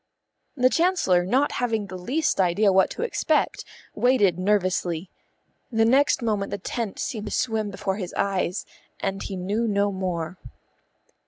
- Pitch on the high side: Yes, high, 200 Hz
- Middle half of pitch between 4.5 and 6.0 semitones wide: No, average, 3.8 semitones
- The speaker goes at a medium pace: Yes, average, 150 wpm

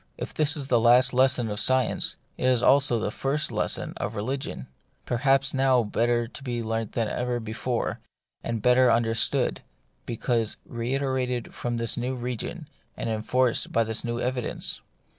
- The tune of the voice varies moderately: No, narrow, 2.1 semitones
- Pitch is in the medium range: No, low, 120 Hz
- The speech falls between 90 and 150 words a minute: No, average, 160 wpm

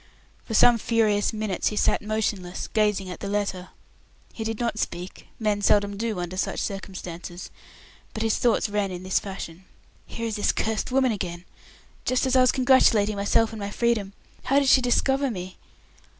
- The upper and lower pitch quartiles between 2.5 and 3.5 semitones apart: Yes, average, 3.1 semitones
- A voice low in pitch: No, high, 210 Hz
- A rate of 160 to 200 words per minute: Yes, average, 180 wpm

